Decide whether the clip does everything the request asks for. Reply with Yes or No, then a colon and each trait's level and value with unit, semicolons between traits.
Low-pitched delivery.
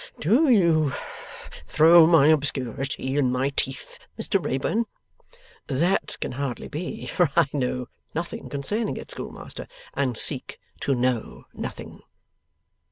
No: medium, 145 Hz